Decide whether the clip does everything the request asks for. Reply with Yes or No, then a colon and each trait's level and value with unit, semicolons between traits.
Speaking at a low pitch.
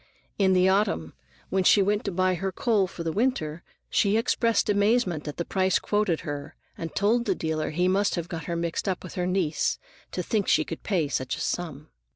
No: medium, 185 Hz